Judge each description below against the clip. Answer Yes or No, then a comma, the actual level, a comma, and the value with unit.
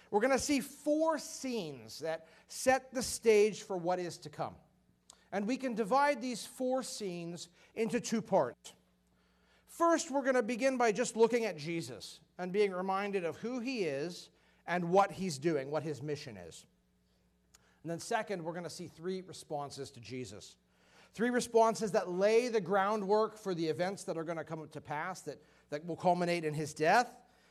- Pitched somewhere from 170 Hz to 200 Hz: Yes, medium, 185 Hz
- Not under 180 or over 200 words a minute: Yes, average, 185 wpm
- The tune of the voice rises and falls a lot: Yes, wide, 6.9 semitones